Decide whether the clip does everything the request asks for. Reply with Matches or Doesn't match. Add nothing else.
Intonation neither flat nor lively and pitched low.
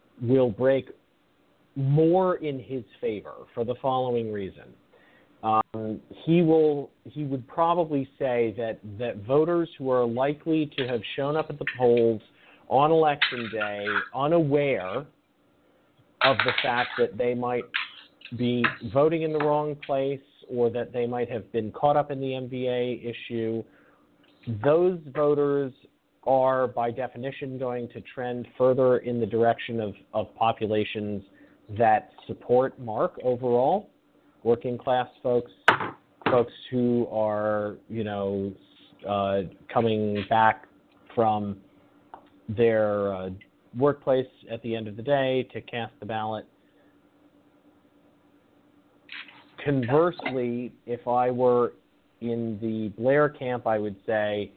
Matches